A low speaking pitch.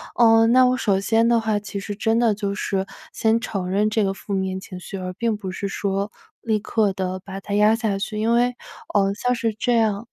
No: high, 210 Hz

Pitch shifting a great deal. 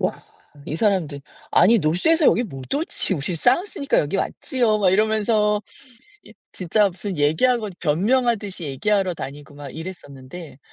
Yes: wide, 6.2 semitones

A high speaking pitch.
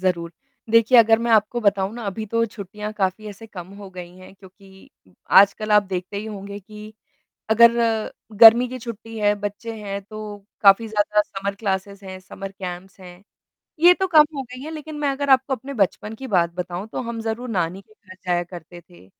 Yes: high, 205 Hz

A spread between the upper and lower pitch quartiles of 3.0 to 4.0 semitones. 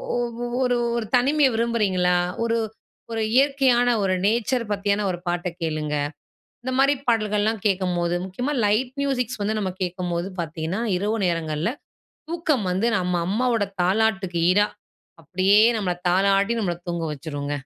No: average, 4.9 semitones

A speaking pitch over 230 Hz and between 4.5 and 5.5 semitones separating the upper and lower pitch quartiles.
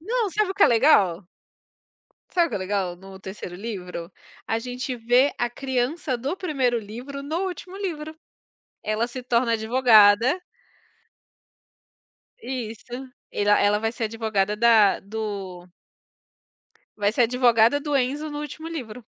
Yes: high, 240 Hz; average, 5.1 semitones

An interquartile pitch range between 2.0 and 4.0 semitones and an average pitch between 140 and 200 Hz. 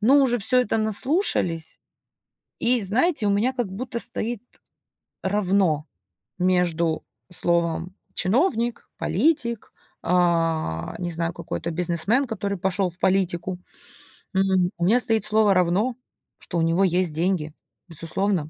No: average, 4.6 semitones; high, 190 Hz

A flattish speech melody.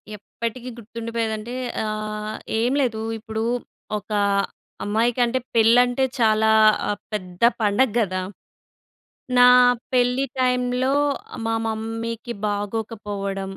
Yes: narrow, 2.3 semitones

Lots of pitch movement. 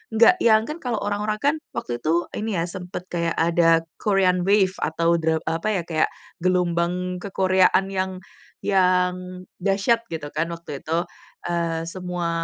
No: narrow, 2.5 semitones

